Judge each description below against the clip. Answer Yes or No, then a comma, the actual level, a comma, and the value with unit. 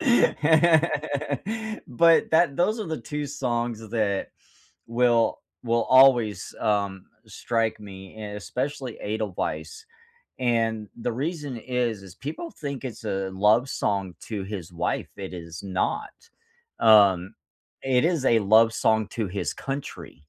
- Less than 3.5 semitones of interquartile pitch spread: No, average, 4.5 semitones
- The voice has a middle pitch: No, low, 115 Hz